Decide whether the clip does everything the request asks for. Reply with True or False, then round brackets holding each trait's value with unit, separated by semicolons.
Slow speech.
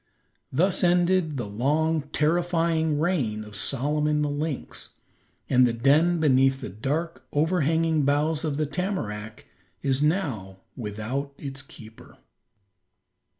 True (115 wpm)